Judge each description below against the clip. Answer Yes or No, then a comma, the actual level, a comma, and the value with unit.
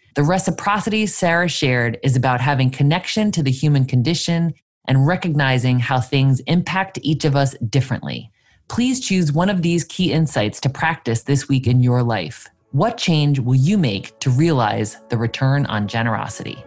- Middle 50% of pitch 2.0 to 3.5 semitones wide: No, average, 5.0 semitones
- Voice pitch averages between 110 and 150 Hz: Yes, medium, 140 Hz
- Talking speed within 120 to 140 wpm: No, average, 165 wpm